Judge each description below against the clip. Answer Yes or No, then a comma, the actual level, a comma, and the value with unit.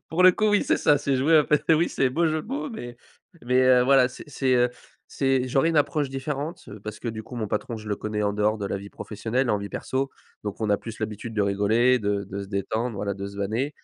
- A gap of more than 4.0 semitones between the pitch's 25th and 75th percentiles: Yes, average, 4.7 semitones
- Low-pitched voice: Yes, low, 120 Hz